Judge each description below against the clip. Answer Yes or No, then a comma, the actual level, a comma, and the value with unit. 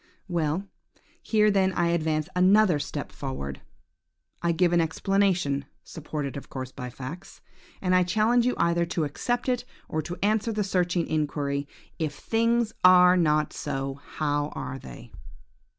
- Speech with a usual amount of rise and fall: Yes, average, 5.0 semitones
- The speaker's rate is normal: Yes, average, 150 wpm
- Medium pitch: Yes, medium, 170 Hz